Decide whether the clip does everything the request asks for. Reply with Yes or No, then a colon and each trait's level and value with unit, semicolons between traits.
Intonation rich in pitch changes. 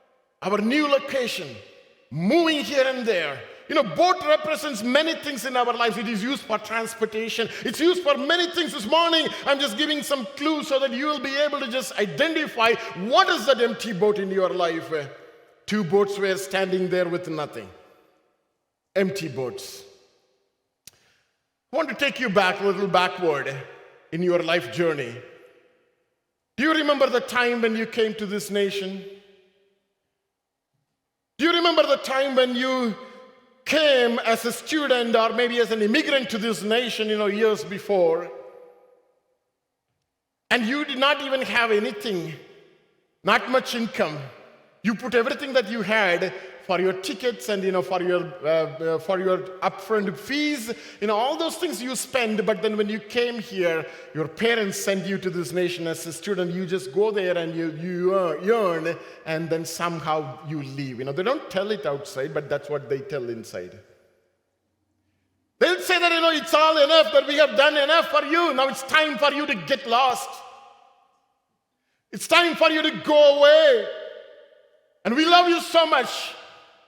Yes: wide, 7.6 semitones